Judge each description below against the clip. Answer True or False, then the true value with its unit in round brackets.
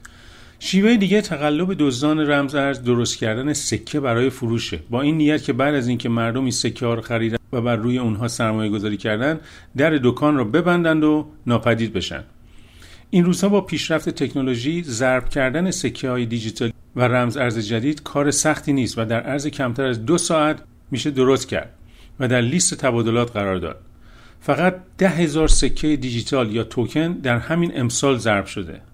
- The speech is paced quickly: True (175 wpm)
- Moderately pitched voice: False (130 Hz)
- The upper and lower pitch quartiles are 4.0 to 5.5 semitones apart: True (4.6 semitones)